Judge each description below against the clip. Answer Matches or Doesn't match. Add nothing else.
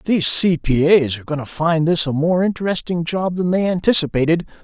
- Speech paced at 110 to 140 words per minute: Doesn't match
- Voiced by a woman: Doesn't match